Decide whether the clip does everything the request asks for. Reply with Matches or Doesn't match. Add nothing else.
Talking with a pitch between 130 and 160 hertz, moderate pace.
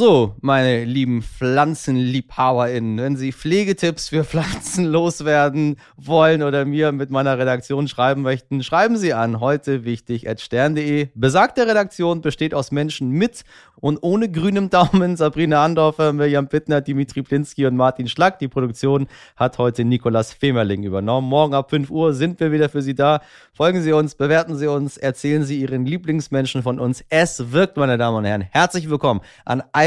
Matches